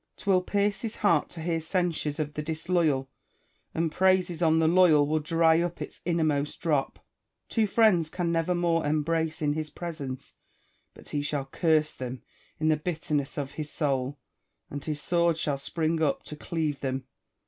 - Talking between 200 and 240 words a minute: No, average, 180 wpm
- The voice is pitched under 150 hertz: No, medium, 160 Hz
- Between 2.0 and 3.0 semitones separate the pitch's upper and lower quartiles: Yes, average, 2.7 semitones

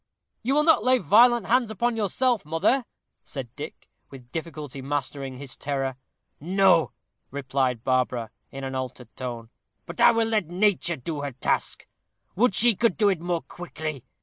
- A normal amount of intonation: No, wide, 8.1 semitones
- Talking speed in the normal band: Yes, average, 160 wpm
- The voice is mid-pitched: Yes, medium, 160 Hz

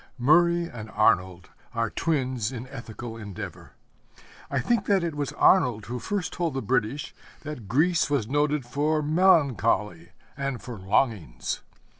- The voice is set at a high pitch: No, low, 130 Hz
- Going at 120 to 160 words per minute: Yes, average, 140 wpm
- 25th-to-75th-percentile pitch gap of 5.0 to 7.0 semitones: Yes, wide, 5.5 semitones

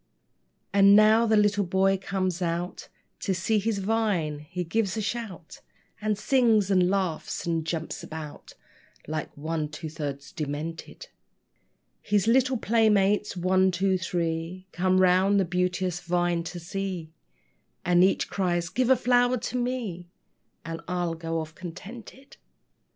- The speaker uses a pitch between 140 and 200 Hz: Yes, medium, 185 Hz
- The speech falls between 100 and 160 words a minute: Yes, average, 140 wpm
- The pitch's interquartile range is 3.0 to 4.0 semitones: Yes, average, 3.7 semitones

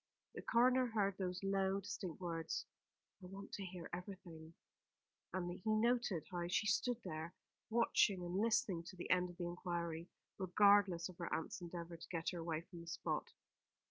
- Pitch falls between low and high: Yes, medium, 180 Hz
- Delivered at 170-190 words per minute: Yes, average, 175 wpm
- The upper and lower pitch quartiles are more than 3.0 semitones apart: No, average, 2.7 semitones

